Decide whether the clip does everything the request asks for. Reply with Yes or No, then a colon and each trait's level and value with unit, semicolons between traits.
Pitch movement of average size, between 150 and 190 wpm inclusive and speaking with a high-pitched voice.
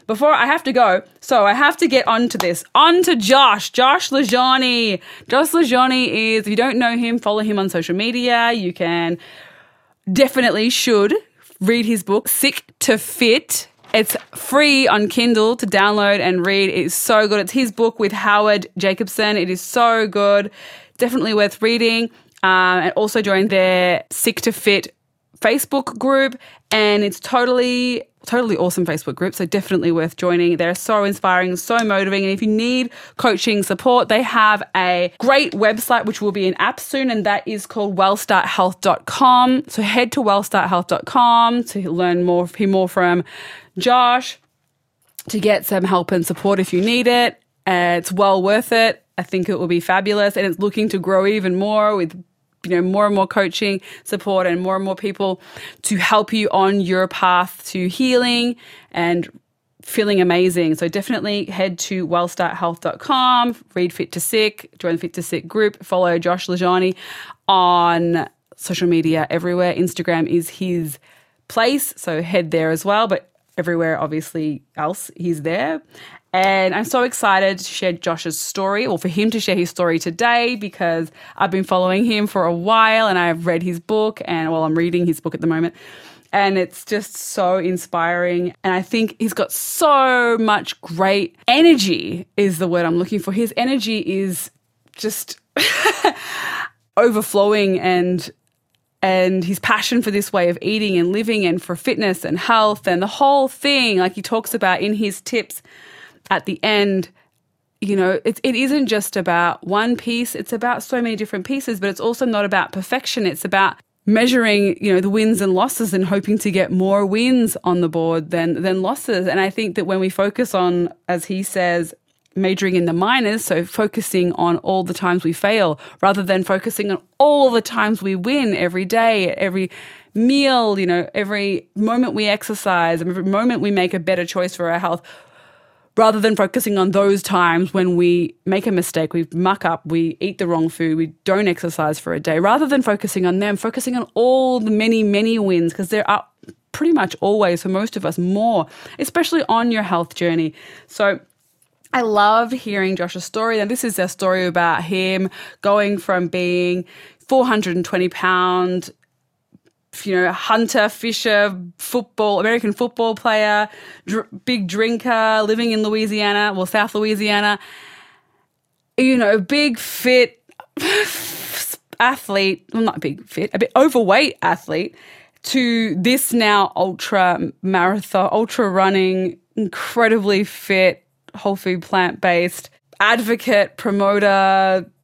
Yes: average, 4.0 semitones; average, 170 wpm; high, 200 Hz